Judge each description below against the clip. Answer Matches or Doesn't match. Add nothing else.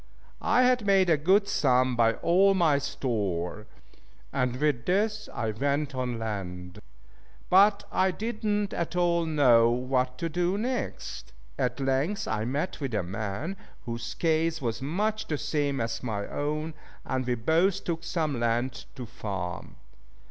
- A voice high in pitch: Doesn't match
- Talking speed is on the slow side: Doesn't match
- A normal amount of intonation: Doesn't match